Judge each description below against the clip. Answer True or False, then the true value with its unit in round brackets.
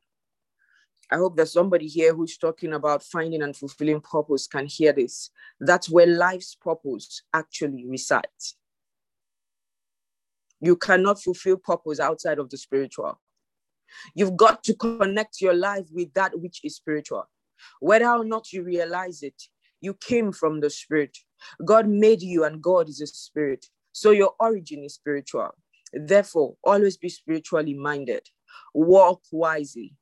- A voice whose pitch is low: False (170 Hz)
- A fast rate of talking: False (140 wpm)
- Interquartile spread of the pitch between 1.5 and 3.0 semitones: False (4.4 semitones)